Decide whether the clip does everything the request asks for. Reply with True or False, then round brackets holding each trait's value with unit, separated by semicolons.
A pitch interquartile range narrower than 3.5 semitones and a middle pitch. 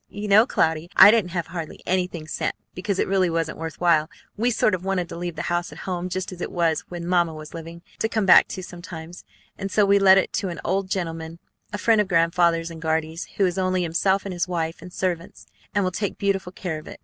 True (2.4 semitones; 180 Hz)